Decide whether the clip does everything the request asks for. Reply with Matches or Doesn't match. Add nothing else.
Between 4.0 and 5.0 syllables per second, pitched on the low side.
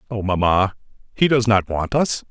Matches